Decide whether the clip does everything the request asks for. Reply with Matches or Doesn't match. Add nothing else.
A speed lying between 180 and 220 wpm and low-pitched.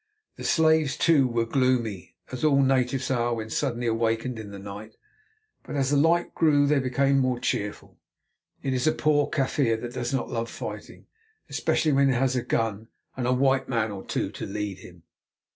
Matches